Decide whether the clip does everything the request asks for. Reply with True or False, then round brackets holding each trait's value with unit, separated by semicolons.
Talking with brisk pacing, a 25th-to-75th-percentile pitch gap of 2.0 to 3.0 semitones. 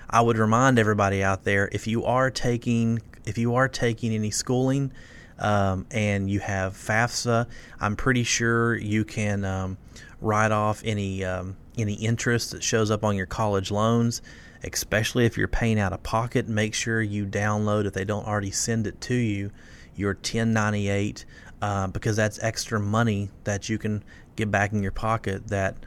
False (175 wpm; 2.5 semitones)